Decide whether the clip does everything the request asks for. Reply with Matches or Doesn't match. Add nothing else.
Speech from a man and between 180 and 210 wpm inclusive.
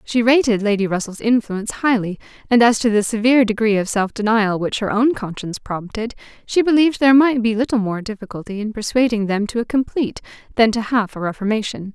Doesn't match